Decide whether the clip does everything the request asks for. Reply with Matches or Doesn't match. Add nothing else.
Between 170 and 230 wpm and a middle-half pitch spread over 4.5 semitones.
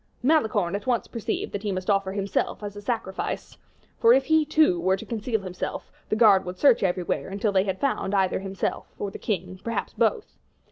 Doesn't match